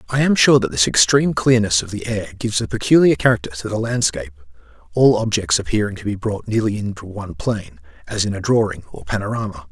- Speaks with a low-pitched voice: Yes, low, 115 Hz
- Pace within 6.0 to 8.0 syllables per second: Yes, 6.4 syllables/s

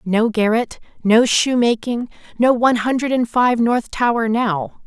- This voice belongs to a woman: Yes, female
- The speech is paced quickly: No, average, 150 wpm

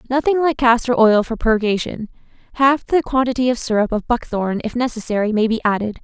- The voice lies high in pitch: Yes, high, 235 Hz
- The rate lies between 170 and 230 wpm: Yes, average, 180 wpm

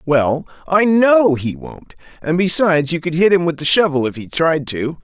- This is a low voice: No, medium, 160 Hz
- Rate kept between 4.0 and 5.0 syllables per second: Yes, 4.7 syllables/s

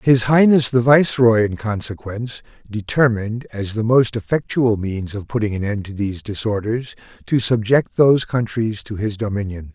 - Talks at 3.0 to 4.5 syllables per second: No, 5.1 syllables/s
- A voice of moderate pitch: No, low, 110 Hz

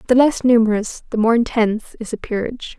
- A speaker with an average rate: Yes, average, 195 wpm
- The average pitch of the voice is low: No, high, 230 Hz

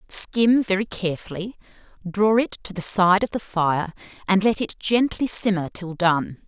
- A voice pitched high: Yes, high, 195 Hz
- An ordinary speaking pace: Yes, average, 165 wpm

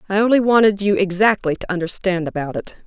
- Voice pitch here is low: No, high, 190 Hz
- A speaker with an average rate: Yes, average, 190 wpm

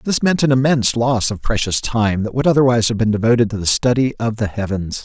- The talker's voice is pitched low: Yes, low, 115 Hz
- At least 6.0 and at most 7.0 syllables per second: Yes, 6.1 syllables/s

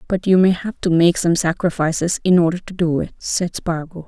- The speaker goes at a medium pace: No, fast, 220 wpm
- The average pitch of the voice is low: No, medium, 175 Hz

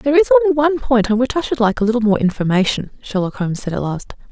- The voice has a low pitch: No, high, 220 Hz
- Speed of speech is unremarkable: No, fast, 265 wpm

